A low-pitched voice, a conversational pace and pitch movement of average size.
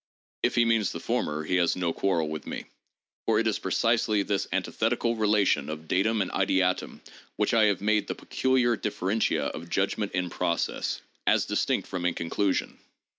Yes: low, 100 Hz; average, 175 wpm; average, 3.6 semitones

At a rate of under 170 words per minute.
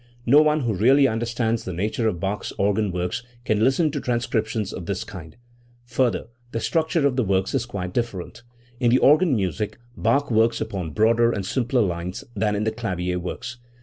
No: average, 190 wpm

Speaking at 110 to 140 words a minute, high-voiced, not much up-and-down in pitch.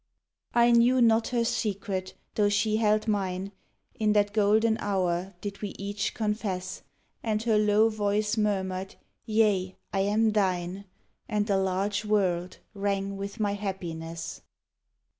Yes: slow, 135 wpm; high, 205 Hz; narrow, 2.0 semitones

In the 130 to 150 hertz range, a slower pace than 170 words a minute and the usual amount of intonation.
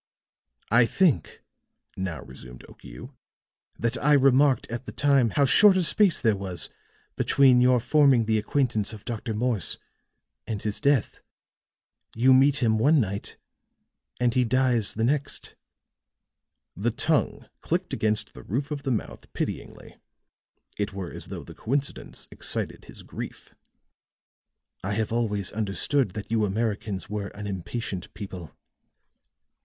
No: low, 115 Hz; average, 140 wpm; average, 4.7 semitones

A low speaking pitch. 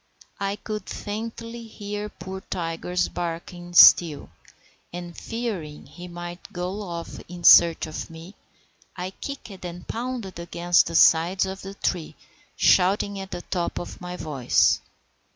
No: medium, 180 Hz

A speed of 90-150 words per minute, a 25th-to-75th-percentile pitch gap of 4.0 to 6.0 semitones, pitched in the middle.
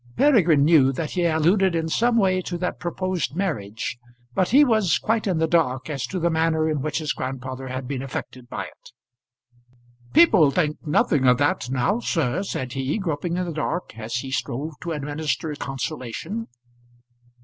No: average, 175 wpm; average, 5.3 semitones; medium, 160 Hz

